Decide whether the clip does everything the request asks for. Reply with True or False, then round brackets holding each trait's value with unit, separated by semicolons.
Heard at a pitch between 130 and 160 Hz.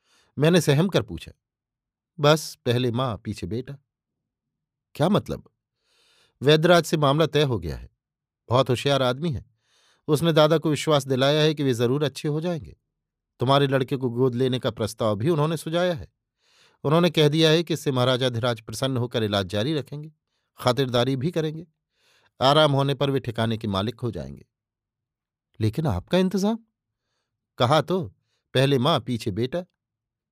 True (135 Hz)